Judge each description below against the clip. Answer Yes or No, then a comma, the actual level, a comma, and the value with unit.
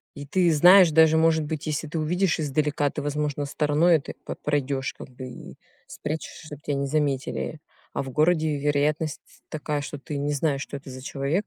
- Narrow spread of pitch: Yes, narrow, 2.0 semitones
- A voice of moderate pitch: Yes, medium, 150 Hz